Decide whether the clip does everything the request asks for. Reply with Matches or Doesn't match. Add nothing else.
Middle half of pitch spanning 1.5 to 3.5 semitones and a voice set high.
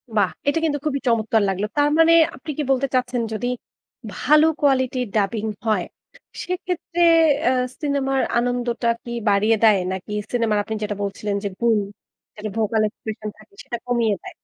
Doesn't match